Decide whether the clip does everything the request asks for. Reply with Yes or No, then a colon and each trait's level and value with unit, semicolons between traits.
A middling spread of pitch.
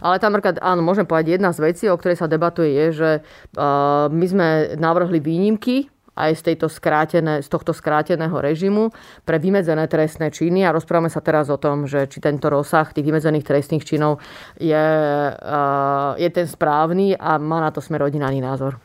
No: narrow, 2.3 semitones